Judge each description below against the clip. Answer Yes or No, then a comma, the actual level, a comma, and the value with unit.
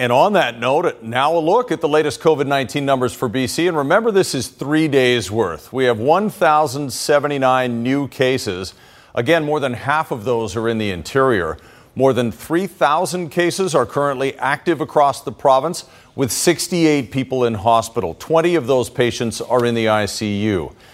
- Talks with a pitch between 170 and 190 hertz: No, low, 135 Hz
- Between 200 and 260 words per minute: No, average, 170 wpm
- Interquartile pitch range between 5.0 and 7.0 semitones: No, average, 4.3 semitones